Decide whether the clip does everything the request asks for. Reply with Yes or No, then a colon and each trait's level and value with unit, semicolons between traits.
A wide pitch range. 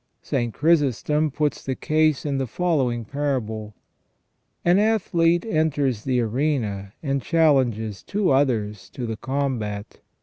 Yes: wide, 5.7 semitones